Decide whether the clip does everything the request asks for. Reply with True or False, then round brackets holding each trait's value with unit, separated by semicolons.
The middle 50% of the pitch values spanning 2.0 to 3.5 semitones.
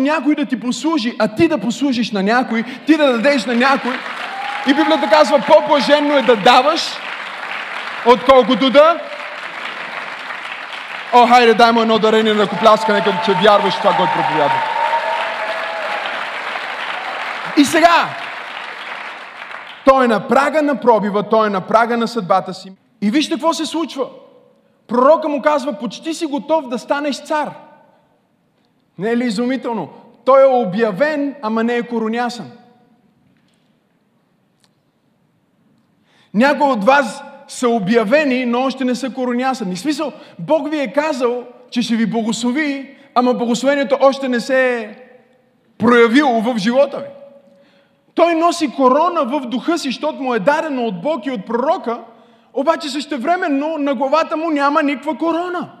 False (3.9 semitones)